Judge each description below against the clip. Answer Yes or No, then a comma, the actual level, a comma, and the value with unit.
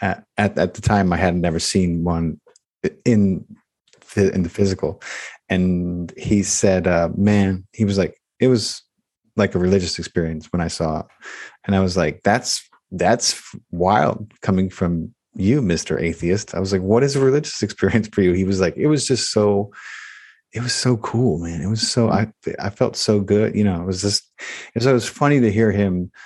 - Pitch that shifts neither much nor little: Yes, average, 3.7 semitones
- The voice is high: No, low, 100 Hz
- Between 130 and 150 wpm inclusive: No, average, 200 wpm